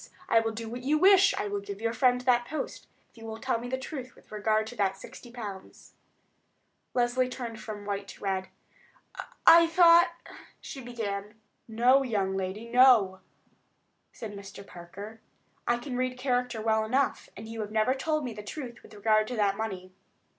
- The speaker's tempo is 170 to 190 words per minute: Yes, average, 175 wpm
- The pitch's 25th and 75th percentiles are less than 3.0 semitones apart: No, average, 3.4 semitones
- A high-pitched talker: Yes, high, 225 Hz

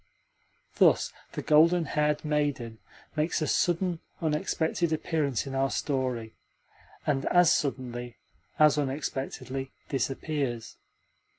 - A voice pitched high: No, medium, 145 Hz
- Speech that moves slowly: Yes, slow, 100 wpm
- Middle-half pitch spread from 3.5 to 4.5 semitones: No, average, 2.8 semitones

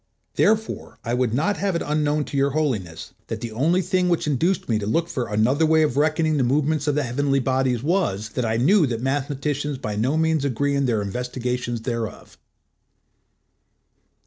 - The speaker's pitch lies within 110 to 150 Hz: Yes, medium, 140 Hz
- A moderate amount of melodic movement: Yes, average, 4.4 semitones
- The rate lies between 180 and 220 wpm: Yes, average, 185 wpm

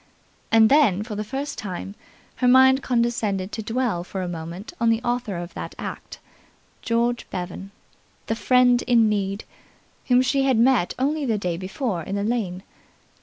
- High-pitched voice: Yes, high, 225 Hz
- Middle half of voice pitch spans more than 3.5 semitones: Yes, average, 4.5 semitones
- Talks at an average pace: Yes, average, 170 wpm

